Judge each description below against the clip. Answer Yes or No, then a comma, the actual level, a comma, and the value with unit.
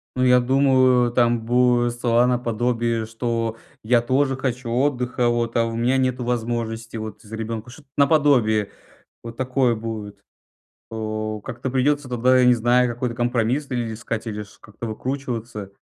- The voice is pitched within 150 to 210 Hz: No, low, 120 Hz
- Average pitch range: No, narrow, 2.0 semitones